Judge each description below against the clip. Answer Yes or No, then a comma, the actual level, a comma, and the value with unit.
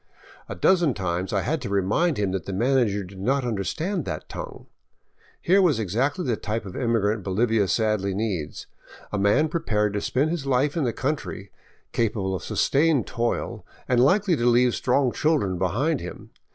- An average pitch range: No, wide, 6.0 semitones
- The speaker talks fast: No, average, 180 wpm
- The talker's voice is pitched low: Yes, low, 115 Hz